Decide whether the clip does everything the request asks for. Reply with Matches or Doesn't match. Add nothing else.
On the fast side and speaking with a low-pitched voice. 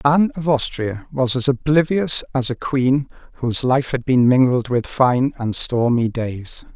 Doesn't match